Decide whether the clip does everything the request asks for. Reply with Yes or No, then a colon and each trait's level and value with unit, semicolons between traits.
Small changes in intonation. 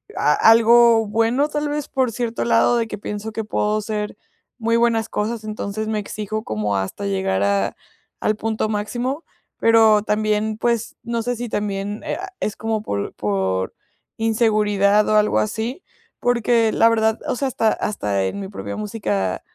Yes: narrow, 2.0 semitones